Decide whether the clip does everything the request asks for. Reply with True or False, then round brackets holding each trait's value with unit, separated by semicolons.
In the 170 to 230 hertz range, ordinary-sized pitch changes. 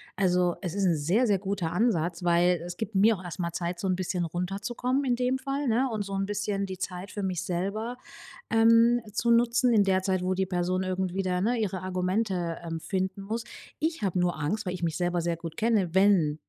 True (190 Hz; 3.6 semitones)